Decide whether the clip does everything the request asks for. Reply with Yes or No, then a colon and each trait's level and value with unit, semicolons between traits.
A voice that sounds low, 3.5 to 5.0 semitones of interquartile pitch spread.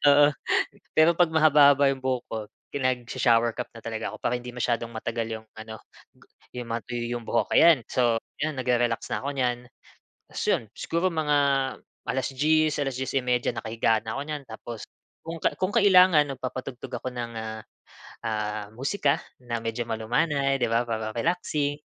Yes: low, 125 Hz; average, 3.9 semitones